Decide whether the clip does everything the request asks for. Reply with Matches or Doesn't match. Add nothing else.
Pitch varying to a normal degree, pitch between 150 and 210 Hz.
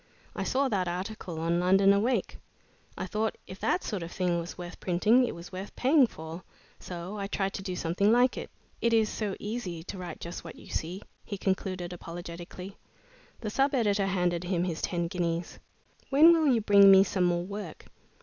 Matches